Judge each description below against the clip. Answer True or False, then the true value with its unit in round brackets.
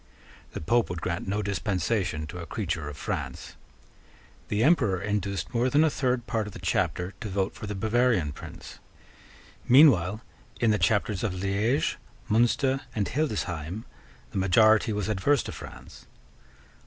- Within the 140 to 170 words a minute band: True (155 wpm)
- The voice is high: False (105 Hz)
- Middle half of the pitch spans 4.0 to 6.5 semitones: True (4.3 semitones)